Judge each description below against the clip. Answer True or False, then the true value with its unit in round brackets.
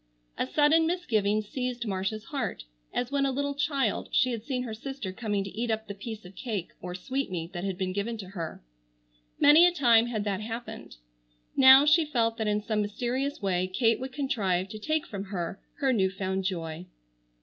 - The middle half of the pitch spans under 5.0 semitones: False (5.4 semitones)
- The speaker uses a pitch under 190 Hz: False (220 Hz)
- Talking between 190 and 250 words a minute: True (195 wpm)